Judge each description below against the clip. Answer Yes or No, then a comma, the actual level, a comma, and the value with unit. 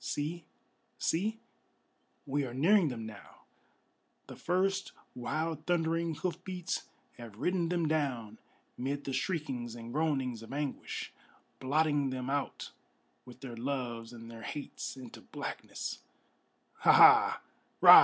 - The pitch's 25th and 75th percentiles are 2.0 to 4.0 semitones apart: No, average, 5.1 semitones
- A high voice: No, medium, 140 Hz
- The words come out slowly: Yes, slow, 125 wpm